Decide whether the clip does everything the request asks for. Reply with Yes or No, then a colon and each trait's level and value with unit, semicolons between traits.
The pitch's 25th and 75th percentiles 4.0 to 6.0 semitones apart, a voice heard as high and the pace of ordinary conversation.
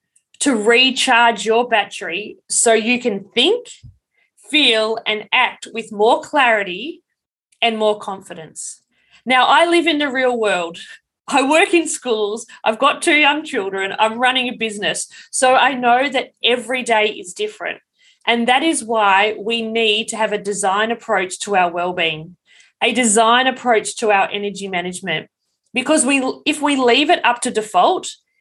Yes: average, 4.8 semitones; high, 235 Hz; average, 160 wpm